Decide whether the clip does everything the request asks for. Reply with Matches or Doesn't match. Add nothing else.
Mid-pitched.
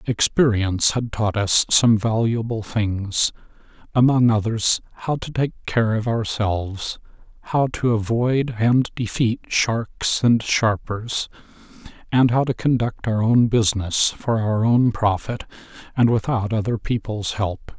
Doesn't match